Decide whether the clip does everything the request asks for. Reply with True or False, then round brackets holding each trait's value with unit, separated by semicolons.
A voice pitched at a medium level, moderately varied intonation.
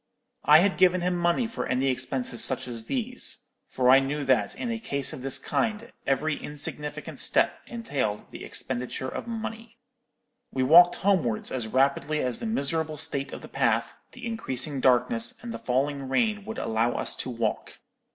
False (145 Hz; 8.4 semitones)